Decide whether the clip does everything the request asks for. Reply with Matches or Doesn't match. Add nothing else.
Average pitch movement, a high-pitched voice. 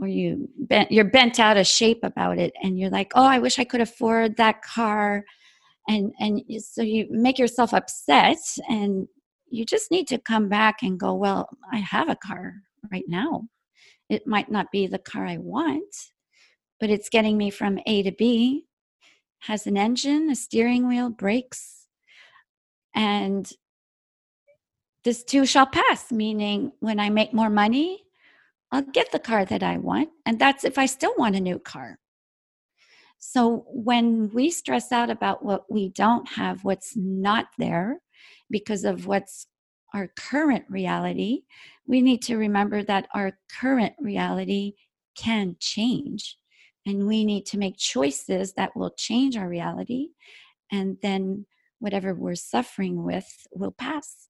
Matches